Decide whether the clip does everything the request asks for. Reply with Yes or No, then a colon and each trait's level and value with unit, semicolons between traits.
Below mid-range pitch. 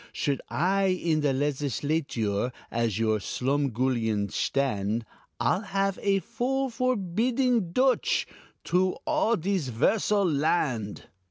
No: medium, 155 Hz